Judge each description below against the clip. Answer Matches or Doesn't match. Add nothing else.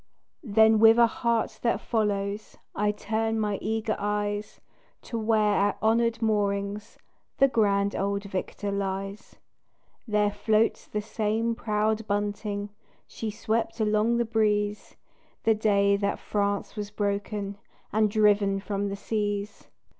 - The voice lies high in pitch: Matches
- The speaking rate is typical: Doesn't match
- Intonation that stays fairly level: Matches